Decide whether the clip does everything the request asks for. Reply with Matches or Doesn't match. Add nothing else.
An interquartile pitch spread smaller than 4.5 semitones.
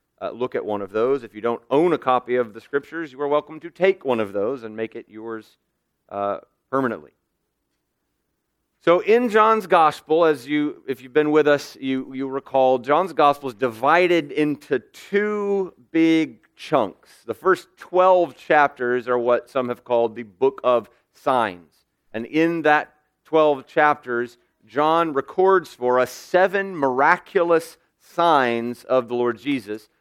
Doesn't match